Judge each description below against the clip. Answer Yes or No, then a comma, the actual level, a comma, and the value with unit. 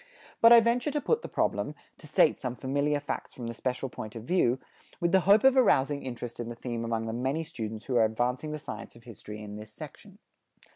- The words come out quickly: Yes, fast, 230 wpm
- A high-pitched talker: No, low, 130 Hz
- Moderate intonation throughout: No, wide, 6.2 semitones